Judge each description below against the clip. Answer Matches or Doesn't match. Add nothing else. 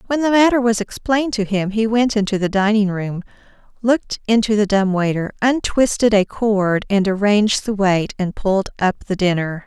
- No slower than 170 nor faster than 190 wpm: Matches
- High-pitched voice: Matches